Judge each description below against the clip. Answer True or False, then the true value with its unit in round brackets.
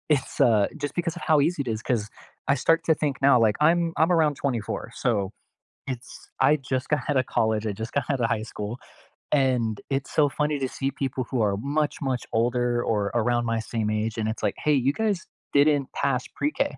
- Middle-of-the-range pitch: False (130 Hz)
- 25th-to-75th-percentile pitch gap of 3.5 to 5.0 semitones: True (4.5 semitones)